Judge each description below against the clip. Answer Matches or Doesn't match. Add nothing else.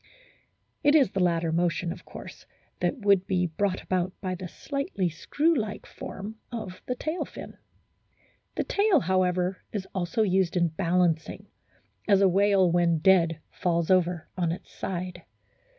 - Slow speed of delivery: Doesn't match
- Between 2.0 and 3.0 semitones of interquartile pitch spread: Matches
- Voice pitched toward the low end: Doesn't match